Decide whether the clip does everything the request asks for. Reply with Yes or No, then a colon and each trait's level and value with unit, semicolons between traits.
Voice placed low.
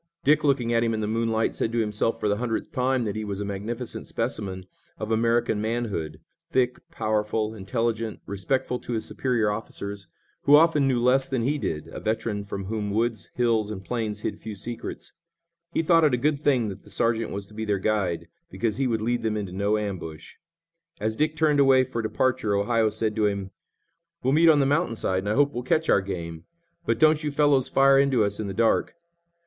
Yes: low, 115 Hz